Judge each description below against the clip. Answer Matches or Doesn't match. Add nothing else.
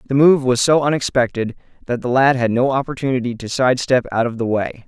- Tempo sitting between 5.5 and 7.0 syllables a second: Matches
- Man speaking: Matches